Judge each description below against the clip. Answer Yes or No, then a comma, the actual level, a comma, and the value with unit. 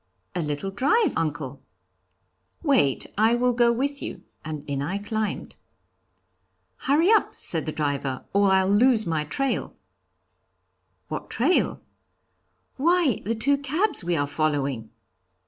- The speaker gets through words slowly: Yes, slow, 130 wpm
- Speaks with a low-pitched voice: No, high, 205 Hz